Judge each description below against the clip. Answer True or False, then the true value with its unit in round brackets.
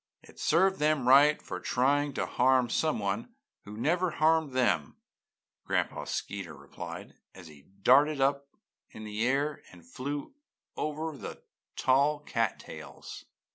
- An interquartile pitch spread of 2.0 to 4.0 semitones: False (5.4 semitones)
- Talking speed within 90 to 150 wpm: True (135 wpm)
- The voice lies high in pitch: False (135 Hz)